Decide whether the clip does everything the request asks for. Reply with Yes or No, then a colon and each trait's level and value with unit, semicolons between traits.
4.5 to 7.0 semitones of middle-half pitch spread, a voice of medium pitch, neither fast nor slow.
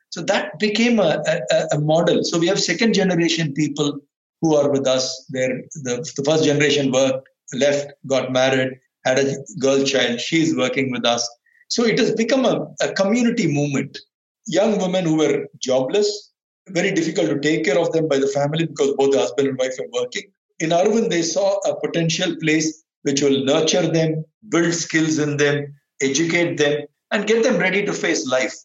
Yes: average, 4.9 semitones; medium, 155 Hz; average, 185 wpm